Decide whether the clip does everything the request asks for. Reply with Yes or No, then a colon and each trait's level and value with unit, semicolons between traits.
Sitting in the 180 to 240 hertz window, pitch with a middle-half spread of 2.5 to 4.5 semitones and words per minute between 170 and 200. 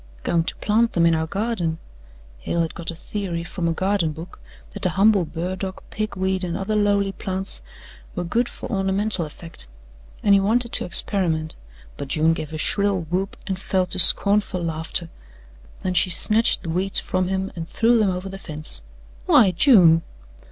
Yes: medium, 185 Hz; average, 3.1 semitones; average, 180 wpm